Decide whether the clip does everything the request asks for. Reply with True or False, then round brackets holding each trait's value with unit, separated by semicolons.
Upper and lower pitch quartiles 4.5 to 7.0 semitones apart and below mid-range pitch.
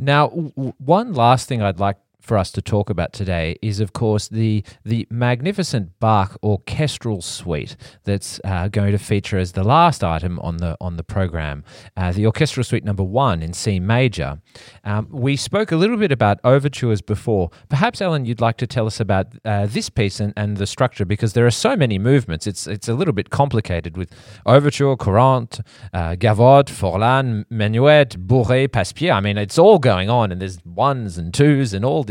True (4.8 semitones; 110 Hz)